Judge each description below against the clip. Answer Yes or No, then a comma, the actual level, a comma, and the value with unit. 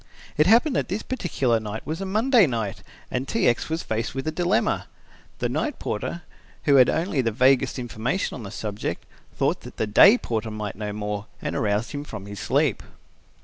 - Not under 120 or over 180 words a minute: No, average, 195 wpm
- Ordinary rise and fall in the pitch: No, wide, 7.6 semitones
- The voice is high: No, low, 125 Hz